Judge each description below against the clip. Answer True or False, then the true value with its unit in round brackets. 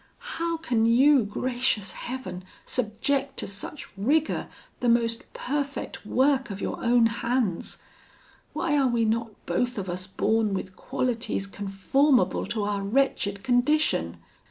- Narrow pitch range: False (4.6 semitones)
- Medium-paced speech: False (130 wpm)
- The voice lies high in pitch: True (235 Hz)